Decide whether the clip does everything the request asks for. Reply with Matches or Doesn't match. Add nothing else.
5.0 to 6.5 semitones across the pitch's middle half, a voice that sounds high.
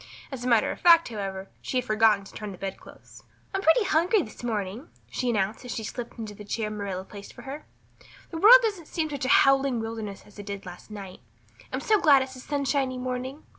Matches